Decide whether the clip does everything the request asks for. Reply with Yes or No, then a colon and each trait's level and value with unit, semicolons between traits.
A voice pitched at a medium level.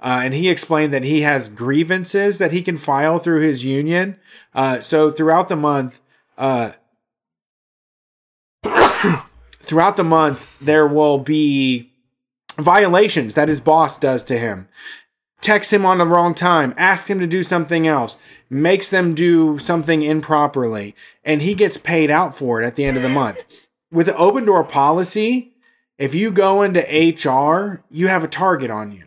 Yes: medium, 155 Hz